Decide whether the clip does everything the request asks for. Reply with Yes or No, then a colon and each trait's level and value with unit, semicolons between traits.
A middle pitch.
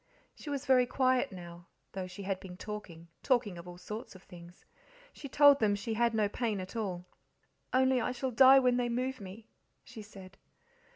No: high, 220 Hz